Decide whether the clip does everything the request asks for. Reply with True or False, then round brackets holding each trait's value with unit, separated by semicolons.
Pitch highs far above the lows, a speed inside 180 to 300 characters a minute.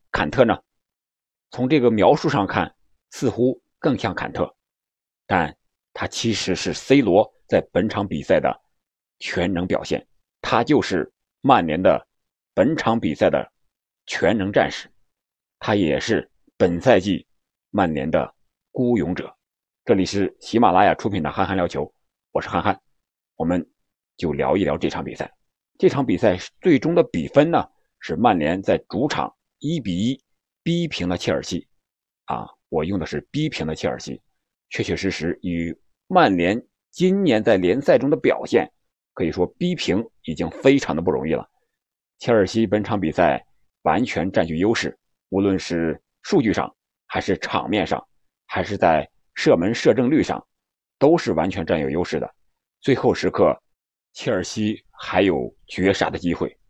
True (6.2 semitones; 225 characters per minute)